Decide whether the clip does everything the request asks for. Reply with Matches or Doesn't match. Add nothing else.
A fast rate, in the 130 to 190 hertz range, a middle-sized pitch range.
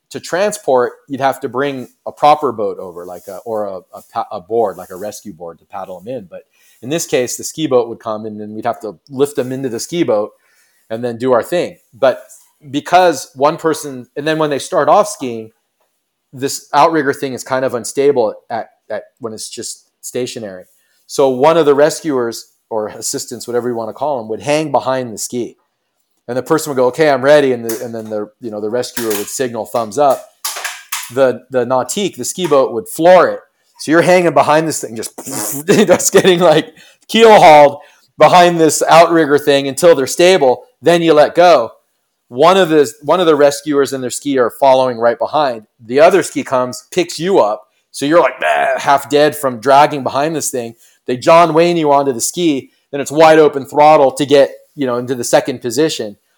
Matches